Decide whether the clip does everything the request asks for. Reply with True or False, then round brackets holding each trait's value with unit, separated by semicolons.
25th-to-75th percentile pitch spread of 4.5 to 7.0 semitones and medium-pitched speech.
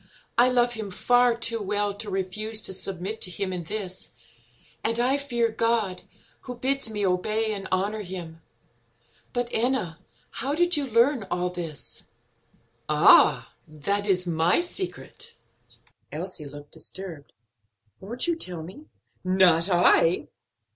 False (4.8 semitones; 205 Hz)